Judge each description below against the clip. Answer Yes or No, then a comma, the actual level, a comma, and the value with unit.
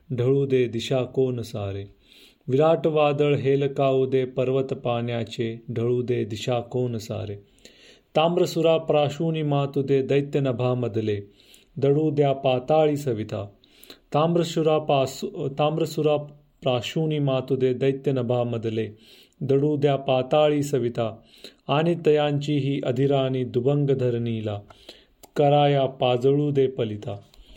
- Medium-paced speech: Yes, average, 100 wpm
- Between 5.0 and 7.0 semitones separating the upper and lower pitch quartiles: No, average, 3.4 semitones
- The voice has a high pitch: No, low, 135 Hz